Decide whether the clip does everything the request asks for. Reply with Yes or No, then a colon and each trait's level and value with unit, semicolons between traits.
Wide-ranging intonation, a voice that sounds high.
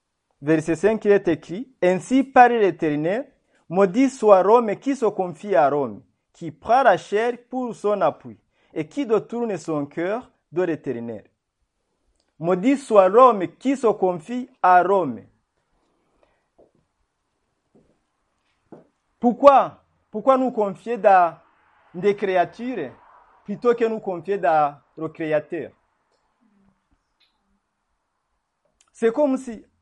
Yes: wide, 6.0 semitones; high, 200 Hz